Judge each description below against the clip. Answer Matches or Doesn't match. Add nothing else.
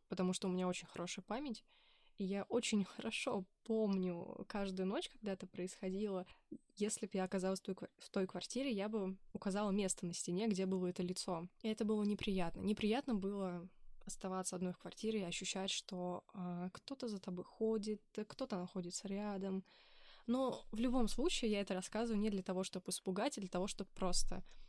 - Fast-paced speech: Matches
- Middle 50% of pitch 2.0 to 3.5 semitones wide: Matches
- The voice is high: Matches